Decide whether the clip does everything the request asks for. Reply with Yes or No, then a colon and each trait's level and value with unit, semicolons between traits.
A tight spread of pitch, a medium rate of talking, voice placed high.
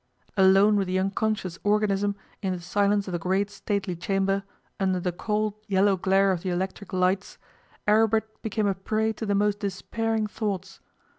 Yes: narrow, 1.7 semitones; average, 165 wpm; high, 200 Hz